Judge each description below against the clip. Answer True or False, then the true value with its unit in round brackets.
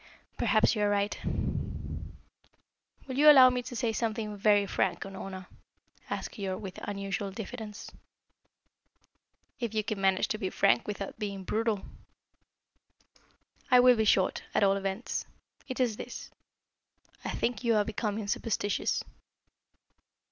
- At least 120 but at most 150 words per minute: True (135 wpm)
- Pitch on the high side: True (210 Hz)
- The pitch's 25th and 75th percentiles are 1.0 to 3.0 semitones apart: True (2.6 semitones)